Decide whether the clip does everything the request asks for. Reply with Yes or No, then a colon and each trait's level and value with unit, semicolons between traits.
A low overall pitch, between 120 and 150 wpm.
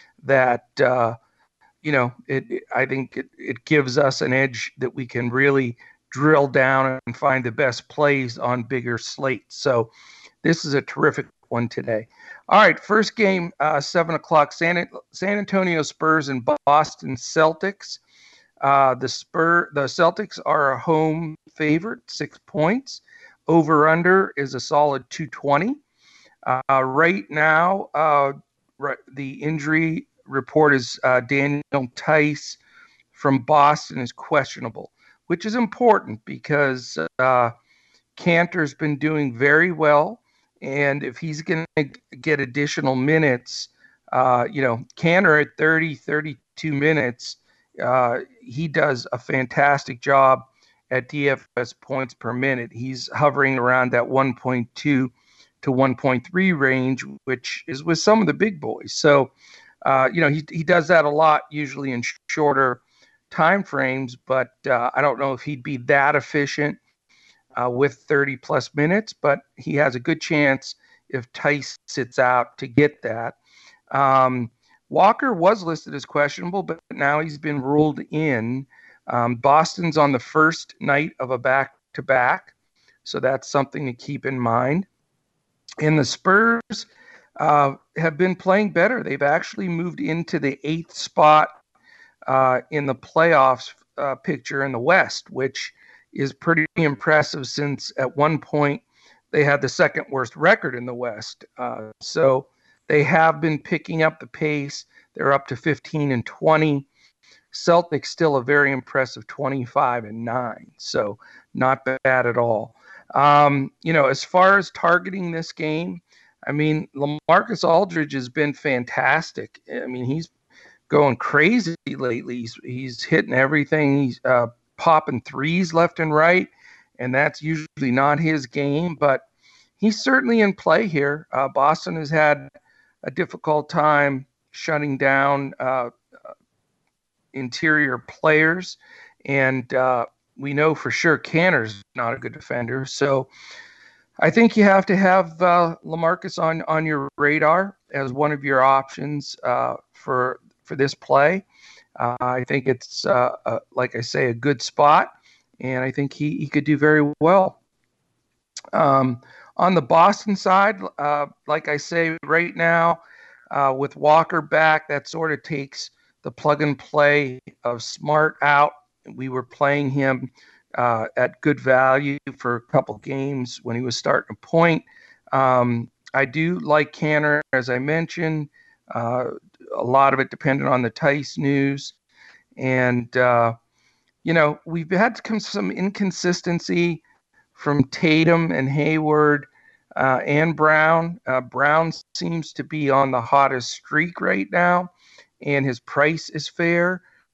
No: medium, 145 Hz; average, 145 wpm